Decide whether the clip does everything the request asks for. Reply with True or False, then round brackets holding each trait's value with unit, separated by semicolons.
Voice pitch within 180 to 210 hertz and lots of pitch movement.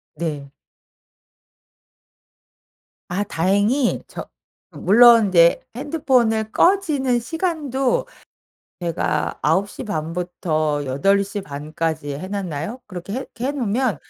True (200 Hz; 7.4 semitones)